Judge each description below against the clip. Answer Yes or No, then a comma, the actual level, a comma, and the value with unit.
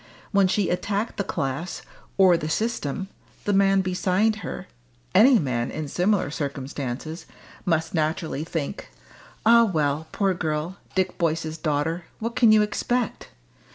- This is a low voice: No, medium, 175 Hz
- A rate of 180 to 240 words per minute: No, slow, 135 wpm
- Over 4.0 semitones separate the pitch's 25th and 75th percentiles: Yes, average, 4.5 semitones